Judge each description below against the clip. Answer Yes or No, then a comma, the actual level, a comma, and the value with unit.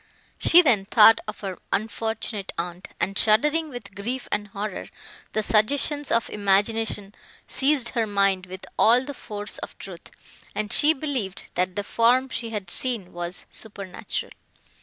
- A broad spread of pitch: No, average, 3.7 semitones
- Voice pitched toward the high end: Yes, high, 215 Hz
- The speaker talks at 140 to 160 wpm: Yes, average, 150 wpm